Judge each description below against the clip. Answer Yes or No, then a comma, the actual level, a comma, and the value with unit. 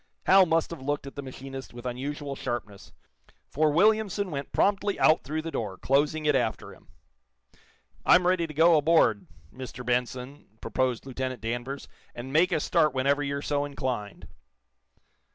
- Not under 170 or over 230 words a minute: No, average, 155 wpm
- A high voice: No, medium, 140 Hz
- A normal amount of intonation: Yes, average, 3.8 semitones